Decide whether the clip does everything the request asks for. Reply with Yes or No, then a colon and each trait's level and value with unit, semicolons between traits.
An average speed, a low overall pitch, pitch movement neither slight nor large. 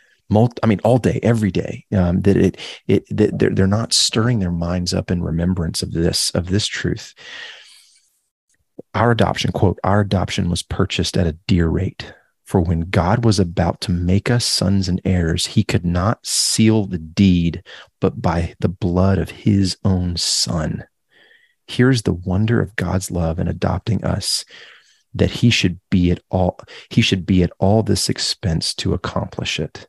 Yes: average, 175 wpm; very low, 95 Hz; average, 3.0 semitones